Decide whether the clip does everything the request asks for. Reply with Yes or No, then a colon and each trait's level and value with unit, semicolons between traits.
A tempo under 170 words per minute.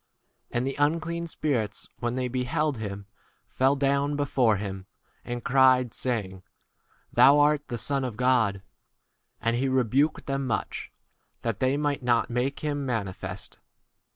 Yes: average, 145 wpm